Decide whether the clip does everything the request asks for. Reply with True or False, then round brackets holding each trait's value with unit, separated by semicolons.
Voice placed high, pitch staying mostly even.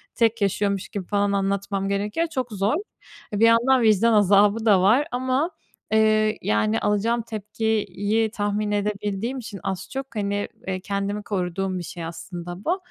True (205 Hz; 2.3 semitones)